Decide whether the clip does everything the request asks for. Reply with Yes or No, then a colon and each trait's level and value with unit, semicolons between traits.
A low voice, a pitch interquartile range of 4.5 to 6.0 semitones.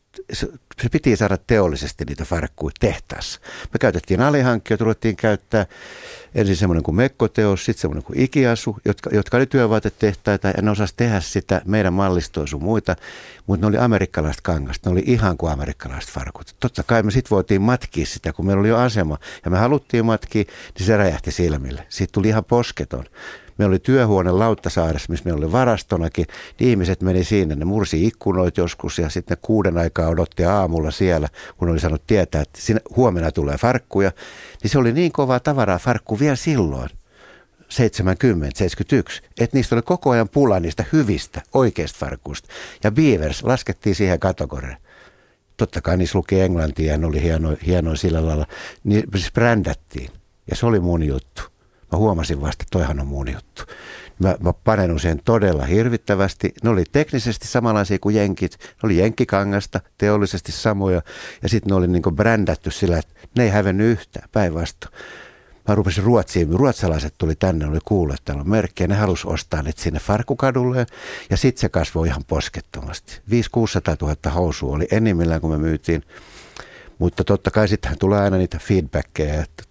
Yes: very low, 95 Hz; average, 5.0 semitones